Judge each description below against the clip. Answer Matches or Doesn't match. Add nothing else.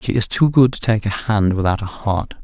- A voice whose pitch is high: Doesn't match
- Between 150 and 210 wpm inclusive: Doesn't match